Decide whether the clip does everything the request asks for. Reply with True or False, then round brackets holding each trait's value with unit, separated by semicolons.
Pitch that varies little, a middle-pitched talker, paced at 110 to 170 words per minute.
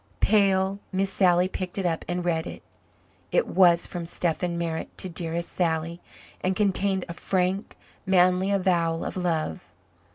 True (2.0 semitones; 180 Hz; 150 wpm)